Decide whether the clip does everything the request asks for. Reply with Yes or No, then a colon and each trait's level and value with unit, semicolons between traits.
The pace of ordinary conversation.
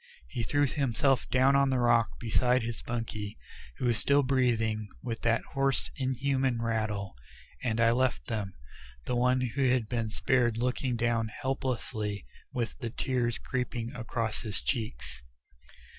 Yes: average, 145 wpm